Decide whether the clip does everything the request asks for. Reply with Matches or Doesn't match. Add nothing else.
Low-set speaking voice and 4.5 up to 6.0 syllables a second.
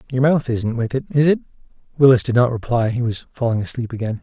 Doesn't match